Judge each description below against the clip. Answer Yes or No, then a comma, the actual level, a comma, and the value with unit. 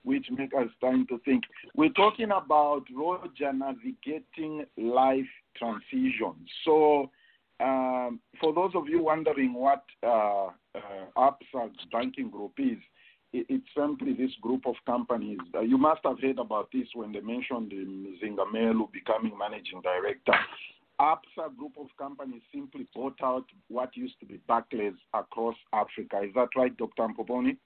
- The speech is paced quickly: No, average, 140 wpm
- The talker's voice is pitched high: No, low, 130 Hz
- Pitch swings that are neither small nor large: No, wide, 5.8 semitones